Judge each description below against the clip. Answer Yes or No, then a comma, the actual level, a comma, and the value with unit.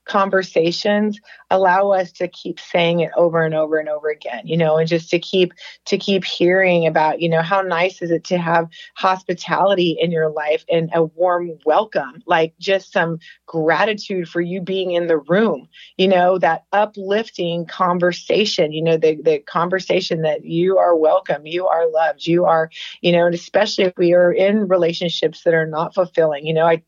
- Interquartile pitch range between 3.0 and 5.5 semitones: No, narrow, 2.6 semitones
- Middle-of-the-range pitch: Yes, medium, 175 Hz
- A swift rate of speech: No, average, 190 wpm